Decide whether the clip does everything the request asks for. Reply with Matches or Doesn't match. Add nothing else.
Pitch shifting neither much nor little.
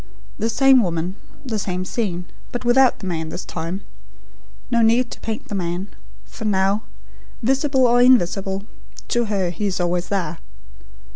Matches